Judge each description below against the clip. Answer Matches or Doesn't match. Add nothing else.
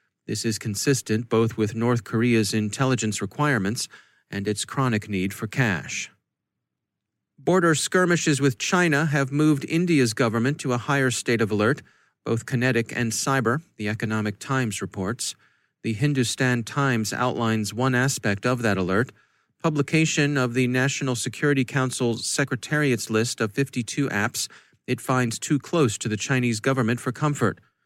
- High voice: Doesn't match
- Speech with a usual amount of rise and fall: Matches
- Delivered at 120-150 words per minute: Matches